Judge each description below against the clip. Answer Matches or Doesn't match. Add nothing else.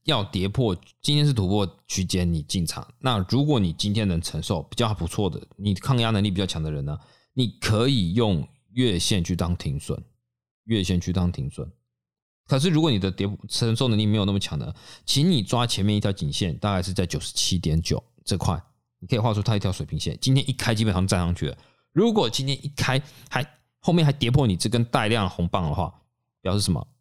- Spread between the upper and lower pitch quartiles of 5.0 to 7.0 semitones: Matches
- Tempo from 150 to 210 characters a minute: Doesn't match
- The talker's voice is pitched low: Matches